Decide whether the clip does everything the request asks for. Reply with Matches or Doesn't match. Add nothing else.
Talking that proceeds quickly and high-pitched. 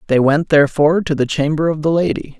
Doesn't match